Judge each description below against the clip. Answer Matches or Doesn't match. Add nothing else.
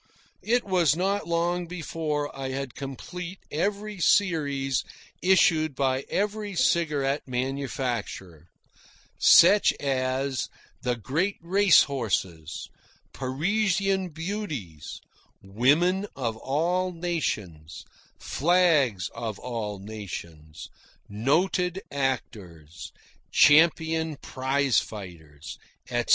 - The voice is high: Doesn't match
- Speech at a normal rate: Doesn't match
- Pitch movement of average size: Doesn't match